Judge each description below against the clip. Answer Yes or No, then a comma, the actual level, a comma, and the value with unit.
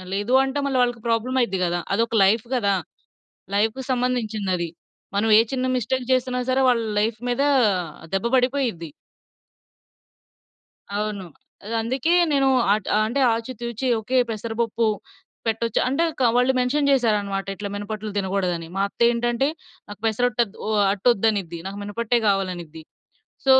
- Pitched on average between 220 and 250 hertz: Yes, high, 225 Hz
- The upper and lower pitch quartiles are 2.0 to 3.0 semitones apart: No, average, 3.7 semitones